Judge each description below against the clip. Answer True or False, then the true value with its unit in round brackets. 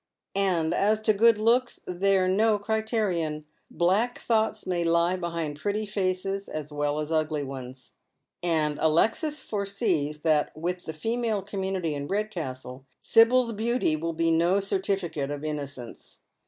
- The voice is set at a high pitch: False (180 Hz)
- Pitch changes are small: False (5.4 semitones)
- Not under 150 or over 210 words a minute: False (140 wpm)